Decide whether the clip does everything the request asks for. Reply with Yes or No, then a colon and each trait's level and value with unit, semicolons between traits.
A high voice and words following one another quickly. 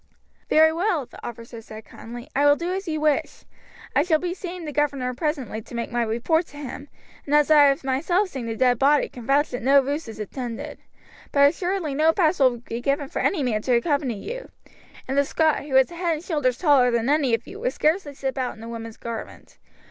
Yes: very high, 280 Hz; fast, 230 wpm